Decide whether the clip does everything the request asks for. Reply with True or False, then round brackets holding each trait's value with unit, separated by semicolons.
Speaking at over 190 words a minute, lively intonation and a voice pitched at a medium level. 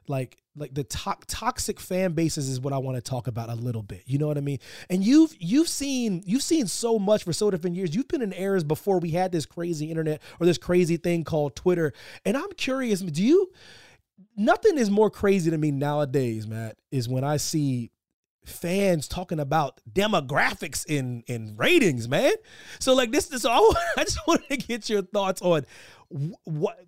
True (200 wpm; 6.6 semitones; 175 Hz)